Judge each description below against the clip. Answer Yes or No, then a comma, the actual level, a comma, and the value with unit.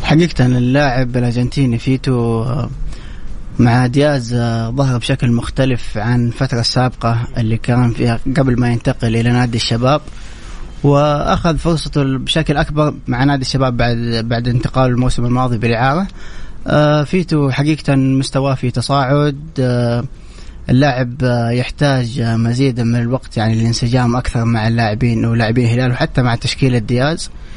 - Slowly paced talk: Yes, slow, 120 wpm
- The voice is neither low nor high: No, low, 125 Hz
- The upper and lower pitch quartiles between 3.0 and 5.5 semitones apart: No, narrow, 2.6 semitones